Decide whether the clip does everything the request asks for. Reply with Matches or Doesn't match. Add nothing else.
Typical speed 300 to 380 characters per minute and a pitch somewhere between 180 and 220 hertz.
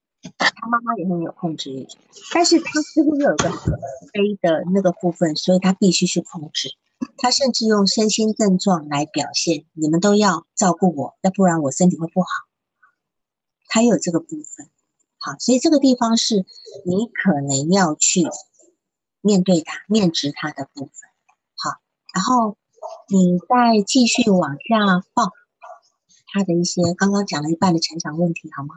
Doesn't match